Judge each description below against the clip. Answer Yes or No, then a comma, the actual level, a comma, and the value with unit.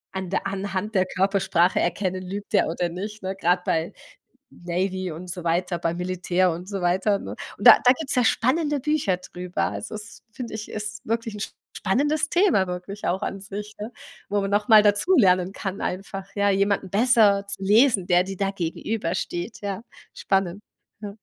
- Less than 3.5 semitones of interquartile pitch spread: Yes, narrow, 2.6 semitones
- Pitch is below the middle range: No, high, 195 Hz